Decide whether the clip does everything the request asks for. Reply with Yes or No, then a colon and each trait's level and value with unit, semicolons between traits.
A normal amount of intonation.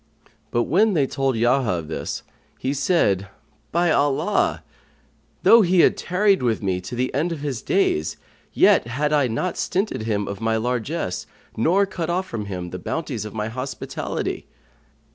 No: wide, 7.7 semitones